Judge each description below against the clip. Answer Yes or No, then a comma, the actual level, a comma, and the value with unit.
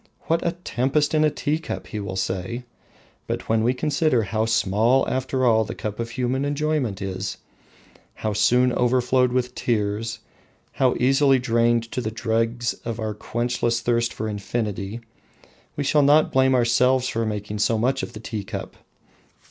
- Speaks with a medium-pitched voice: No, low, 120 Hz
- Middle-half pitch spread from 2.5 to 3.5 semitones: Yes, average, 3.0 semitones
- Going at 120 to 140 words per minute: No, average, 165 wpm